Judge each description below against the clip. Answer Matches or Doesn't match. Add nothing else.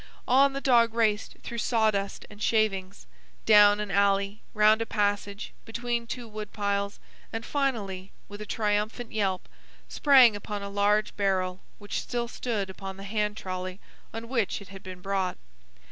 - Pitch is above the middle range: Matches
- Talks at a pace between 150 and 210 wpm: Matches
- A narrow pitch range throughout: Matches